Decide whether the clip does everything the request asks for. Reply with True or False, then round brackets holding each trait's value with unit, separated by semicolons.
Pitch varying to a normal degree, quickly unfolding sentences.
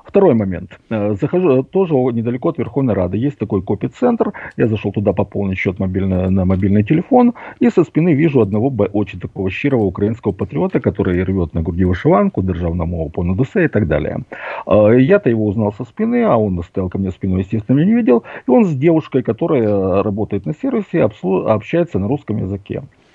False (6.0 semitones; 175 wpm)